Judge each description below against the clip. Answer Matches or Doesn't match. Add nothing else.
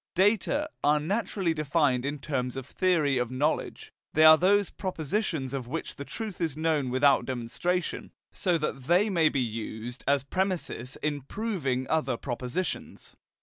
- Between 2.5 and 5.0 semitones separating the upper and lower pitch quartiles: Doesn't match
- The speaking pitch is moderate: Matches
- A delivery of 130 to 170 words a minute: Matches